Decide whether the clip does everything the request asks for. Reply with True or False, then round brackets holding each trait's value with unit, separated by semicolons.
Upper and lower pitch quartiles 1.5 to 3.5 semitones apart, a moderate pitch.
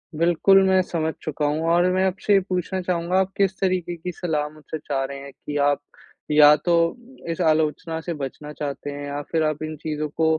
True (3.2 semitones; 160 Hz)